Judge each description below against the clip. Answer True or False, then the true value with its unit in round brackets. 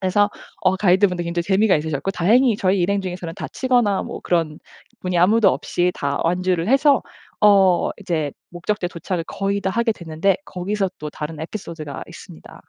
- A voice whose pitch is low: False (185 Hz)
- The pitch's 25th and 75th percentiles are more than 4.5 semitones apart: False (3.1 semitones)